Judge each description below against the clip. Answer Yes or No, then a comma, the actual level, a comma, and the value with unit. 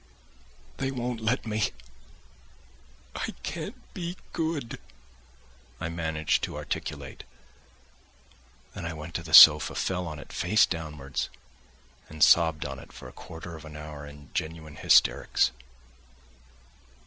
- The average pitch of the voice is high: No, very low, 80 Hz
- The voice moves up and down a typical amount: No, wide, 5.9 semitones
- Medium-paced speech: No, slow, 125 wpm